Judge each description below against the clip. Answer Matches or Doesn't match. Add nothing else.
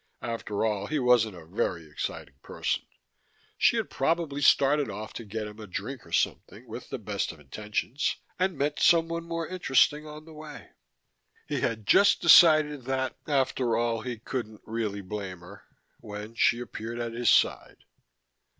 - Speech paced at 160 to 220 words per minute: Matches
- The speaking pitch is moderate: Doesn't match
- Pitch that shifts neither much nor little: Doesn't match